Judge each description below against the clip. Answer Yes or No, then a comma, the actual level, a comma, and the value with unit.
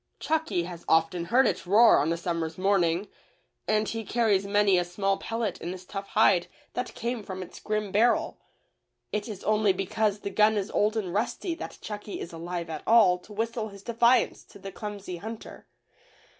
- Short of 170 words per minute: No, average, 185 wpm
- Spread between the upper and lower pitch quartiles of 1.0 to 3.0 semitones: No, average, 3.4 semitones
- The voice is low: No, high, 200 Hz